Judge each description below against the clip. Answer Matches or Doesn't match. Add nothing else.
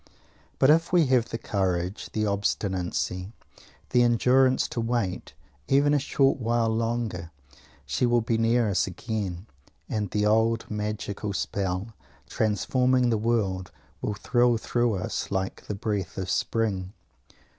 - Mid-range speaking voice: Doesn't match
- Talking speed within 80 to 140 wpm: Matches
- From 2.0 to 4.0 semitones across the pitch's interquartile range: Matches